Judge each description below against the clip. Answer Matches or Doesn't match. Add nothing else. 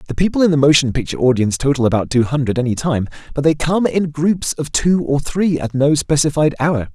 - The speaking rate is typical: Doesn't match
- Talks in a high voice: Doesn't match